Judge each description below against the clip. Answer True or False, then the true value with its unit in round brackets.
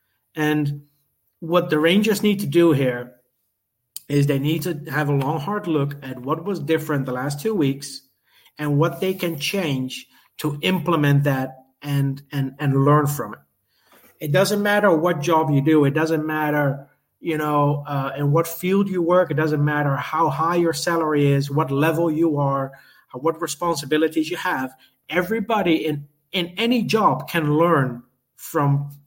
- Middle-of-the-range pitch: True (150 Hz)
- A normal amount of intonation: True (3.2 semitones)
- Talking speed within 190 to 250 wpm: False (165 wpm)